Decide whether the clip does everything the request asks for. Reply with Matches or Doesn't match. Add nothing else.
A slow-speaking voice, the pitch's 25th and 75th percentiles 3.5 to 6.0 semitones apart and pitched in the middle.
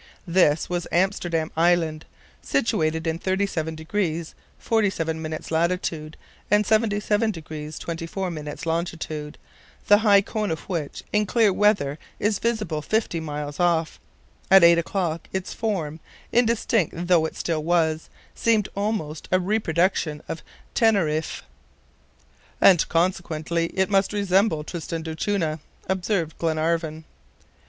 Matches